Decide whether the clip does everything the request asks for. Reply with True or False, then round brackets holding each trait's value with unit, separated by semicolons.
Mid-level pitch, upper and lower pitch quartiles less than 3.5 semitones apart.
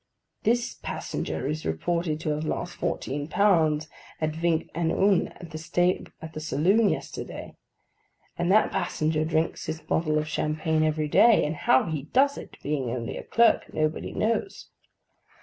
True (160 Hz; 2.5 semitones)